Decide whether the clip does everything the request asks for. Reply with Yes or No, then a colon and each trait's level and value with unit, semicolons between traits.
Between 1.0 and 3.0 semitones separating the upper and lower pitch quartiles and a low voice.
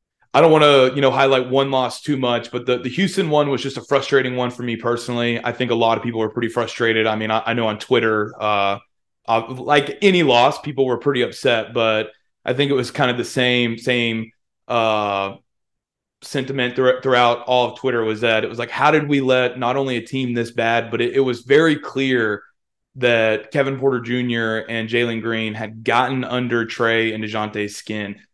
Yes: narrow, 2.6 semitones; low, 120 Hz